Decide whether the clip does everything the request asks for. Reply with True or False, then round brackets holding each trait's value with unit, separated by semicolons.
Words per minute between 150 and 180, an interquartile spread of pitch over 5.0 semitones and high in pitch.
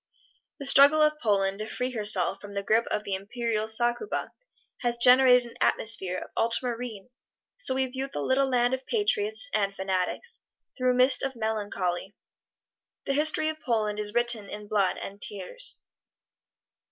False (160 wpm; 4.2 semitones; 235 Hz)